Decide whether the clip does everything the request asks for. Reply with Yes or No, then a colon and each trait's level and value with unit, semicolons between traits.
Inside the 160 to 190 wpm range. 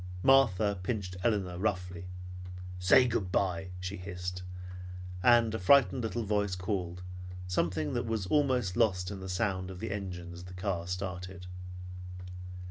No: average, 140 wpm